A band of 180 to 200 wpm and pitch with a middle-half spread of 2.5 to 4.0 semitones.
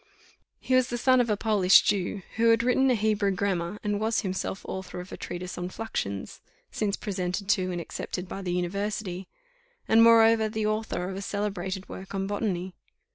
Yes: average, 185 wpm; average, 3.0 semitones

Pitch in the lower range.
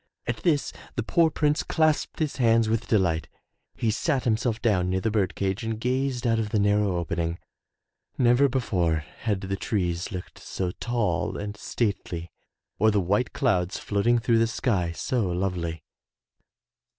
Yes: low, 105 Hz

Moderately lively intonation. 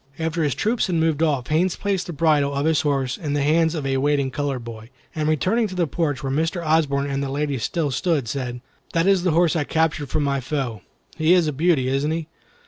Yes: average, 3.1 semitones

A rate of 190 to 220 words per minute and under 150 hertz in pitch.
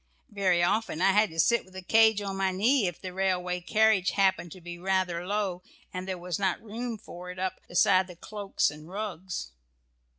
No: average, 200 wpm; high, 190 Hz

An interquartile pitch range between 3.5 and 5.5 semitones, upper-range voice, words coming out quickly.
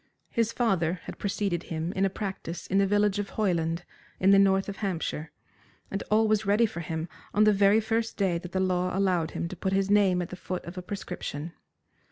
No: average, 2.8 semitones; high, 195 Hz; fast, 220 wpm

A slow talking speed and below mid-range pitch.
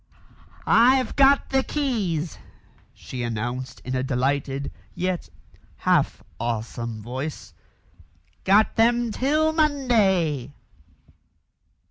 No: slow, 85 wpm; medium, 170 Hz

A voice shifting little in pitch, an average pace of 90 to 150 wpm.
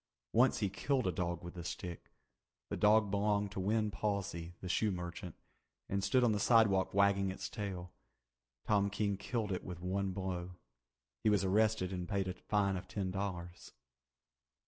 No: narrow, 2.3 semitones; average, 170 wpm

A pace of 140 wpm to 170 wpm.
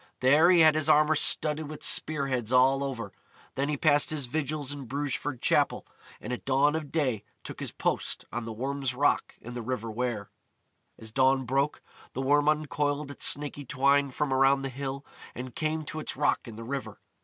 No: average, 195 wpm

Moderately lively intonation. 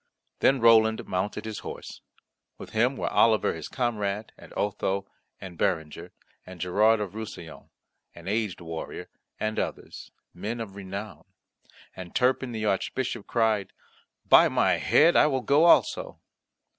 Yes: average, 3.4 semitones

